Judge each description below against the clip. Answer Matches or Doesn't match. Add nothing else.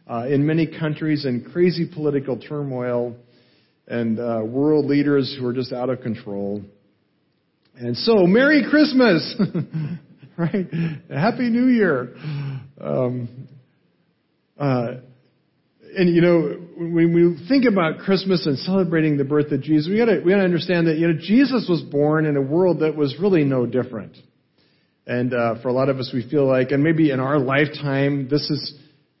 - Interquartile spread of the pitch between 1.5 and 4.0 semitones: Doesn't match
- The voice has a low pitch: Doesn't match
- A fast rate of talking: Doesn't match